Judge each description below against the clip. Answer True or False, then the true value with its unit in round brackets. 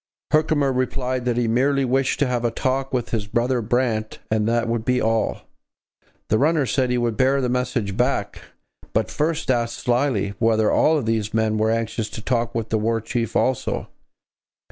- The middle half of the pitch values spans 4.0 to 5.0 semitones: False (2.6 semitones)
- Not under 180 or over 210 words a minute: True (185 wpm)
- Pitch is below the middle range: True (120 Hz)